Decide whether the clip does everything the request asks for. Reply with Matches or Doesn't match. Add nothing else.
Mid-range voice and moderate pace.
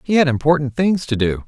Doesn't match